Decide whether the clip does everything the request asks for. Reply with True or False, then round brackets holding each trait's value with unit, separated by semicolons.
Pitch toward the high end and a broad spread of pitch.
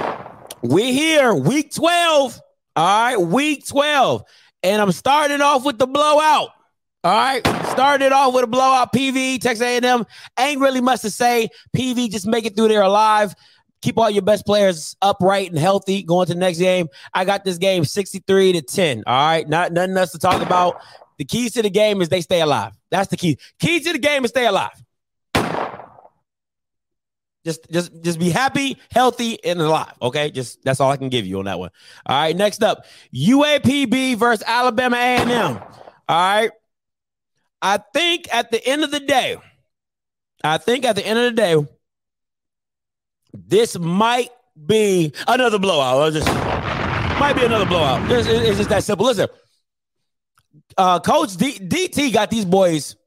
True (215 Hz; 6.1 semitones)